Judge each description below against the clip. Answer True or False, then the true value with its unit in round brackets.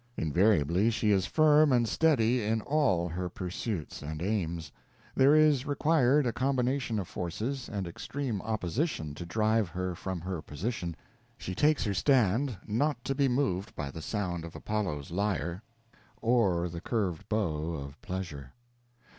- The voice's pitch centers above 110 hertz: False (105 Hz)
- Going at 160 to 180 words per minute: False (150 wpm)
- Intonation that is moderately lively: False (6.5 semitones)